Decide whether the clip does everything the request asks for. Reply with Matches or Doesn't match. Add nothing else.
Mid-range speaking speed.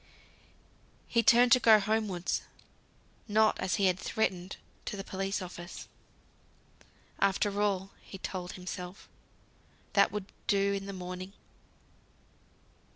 Doesn't match